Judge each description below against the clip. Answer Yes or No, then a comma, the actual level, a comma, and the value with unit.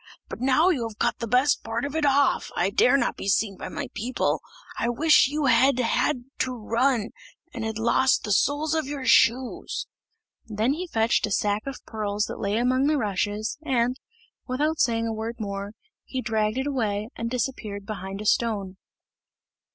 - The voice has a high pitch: Yes, high, 235 Hz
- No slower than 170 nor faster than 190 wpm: Yes, average, 185 wpm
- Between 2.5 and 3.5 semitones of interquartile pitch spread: No, average, 3.9 semitones